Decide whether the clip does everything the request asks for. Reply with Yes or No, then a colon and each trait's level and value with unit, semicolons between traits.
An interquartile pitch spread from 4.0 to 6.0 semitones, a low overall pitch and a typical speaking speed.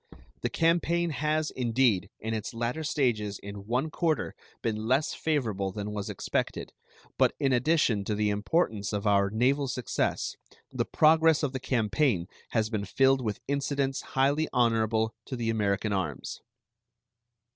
Yes: average, 5.2 semitones; low, 120 Hz; average, 145 wpm